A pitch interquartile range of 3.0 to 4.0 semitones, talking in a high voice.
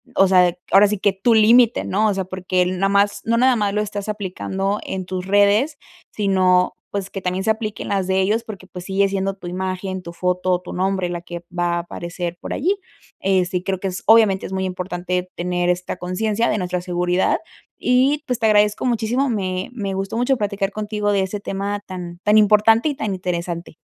No: narrow, 2.5 semitones; high, 195 Hz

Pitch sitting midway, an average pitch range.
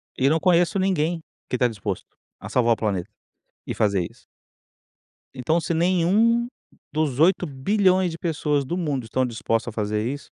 No: medium, 150 Hz; wide, 6.9 semitones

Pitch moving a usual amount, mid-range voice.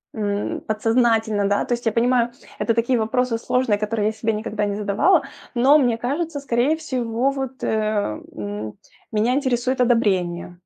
No: average, 3.1 semitones; high, 230 Hz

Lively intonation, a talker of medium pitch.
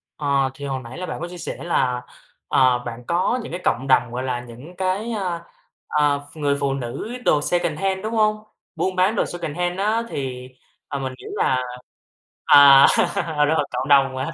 Yes: wide, 5.7 semitones; medium, 145 Hz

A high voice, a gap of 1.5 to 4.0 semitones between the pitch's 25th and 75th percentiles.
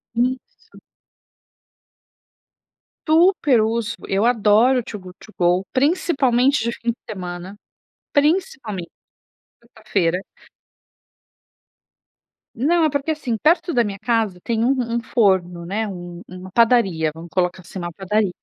No: high, 220 Hz; wide, 5.6 semitones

